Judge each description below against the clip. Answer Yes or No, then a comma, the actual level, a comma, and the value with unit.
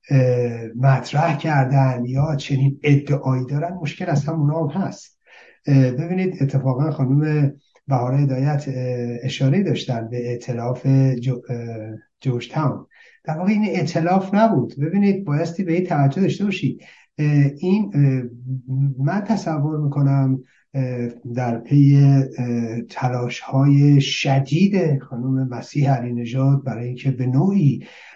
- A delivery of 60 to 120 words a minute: Yes, average, 110 wpm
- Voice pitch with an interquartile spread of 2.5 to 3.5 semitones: Yes, average, 3.1 semitones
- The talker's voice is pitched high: No, low, 135 Hz